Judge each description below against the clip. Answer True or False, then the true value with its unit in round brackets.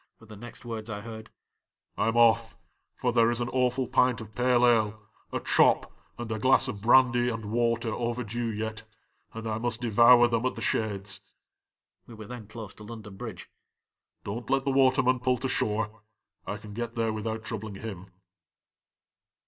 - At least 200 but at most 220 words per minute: False (180 wpm)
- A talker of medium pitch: False (115 Hz)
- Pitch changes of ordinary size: False (1.9 semitones)